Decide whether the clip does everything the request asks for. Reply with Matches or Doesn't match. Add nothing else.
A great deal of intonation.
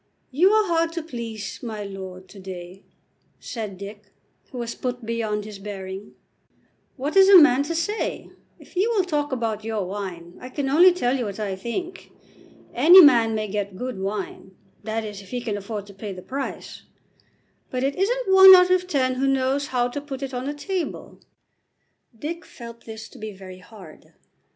Matches